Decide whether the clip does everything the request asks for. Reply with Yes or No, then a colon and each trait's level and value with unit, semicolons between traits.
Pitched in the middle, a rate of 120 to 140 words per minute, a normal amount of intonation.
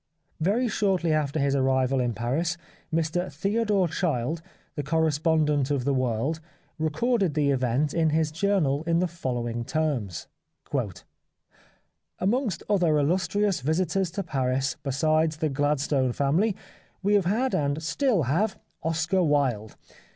Yes: medium, 155 Hz; slow, 135 wpm; average, 4.7 semitones